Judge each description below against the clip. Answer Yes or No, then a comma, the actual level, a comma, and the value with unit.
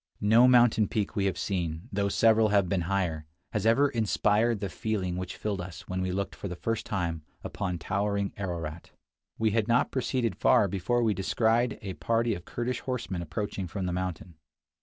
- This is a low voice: Yes, low, 100 Hz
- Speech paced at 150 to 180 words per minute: No, average, 195 wpm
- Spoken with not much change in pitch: No, average, 3.7 semitones